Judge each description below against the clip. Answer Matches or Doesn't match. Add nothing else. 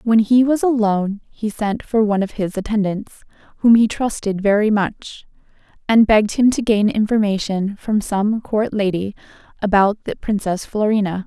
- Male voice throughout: Doesn't match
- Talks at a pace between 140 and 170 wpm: Matches